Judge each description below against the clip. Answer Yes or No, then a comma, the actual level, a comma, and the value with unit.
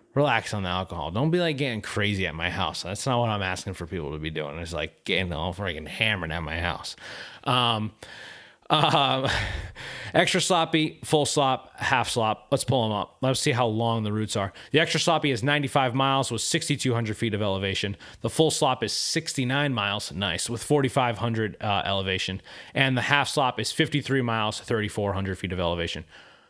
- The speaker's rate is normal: Yes, average, 190 wpm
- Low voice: Yes, low, 115 Hz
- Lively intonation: Yes, wide, 6.1 semitones